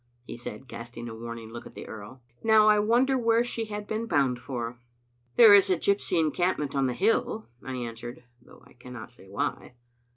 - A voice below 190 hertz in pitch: Yes, low, 135 Hz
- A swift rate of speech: Yes, fast, 215 wpm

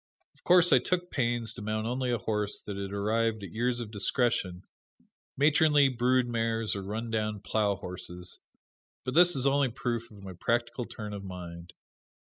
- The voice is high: No, low, 115 Hz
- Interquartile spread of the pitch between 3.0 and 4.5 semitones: Yes, average, 3.6 semitones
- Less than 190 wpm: Yes, average, 175 wpm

